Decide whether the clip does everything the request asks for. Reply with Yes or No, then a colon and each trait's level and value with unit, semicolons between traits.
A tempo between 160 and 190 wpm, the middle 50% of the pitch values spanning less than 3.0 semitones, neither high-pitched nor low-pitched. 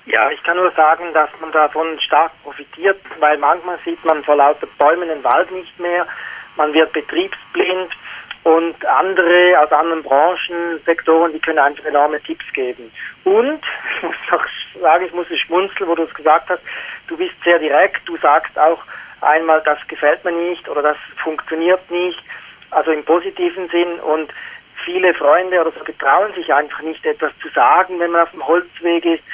Yes: average, 180 wpm; narrow, 2.4 semitones; medium, 165 Hz